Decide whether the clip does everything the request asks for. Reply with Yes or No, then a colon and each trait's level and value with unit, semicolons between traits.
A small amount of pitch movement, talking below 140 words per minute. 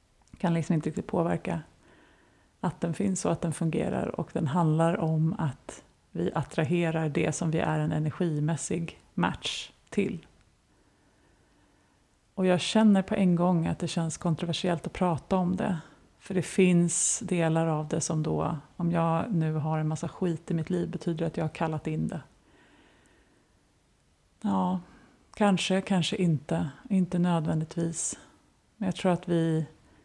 No: narrow, 2.1 semitones; average, 155 wpm